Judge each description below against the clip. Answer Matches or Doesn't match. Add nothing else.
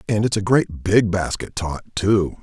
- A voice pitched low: Matches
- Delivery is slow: Doesn't match